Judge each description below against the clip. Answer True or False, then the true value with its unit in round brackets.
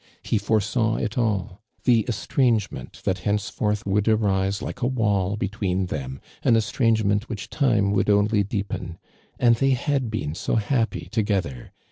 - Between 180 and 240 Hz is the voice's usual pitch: False (105 Hz)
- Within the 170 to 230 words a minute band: False (150 wpm)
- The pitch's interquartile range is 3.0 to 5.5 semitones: False (2.6 semitones)